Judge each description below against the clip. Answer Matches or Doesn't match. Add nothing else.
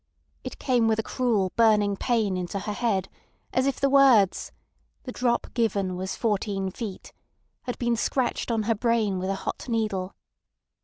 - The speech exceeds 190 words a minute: Doesn't match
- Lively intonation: Doesn't match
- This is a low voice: Doesn't match